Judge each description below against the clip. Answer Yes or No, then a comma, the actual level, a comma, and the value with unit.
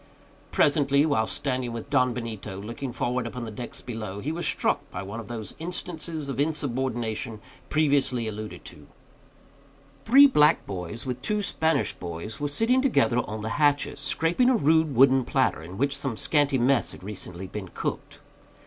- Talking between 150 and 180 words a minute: Yes, average, 165 wpm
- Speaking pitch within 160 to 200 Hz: No, low, 130 Hz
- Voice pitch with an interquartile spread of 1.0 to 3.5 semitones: No, average, 5.2 semitones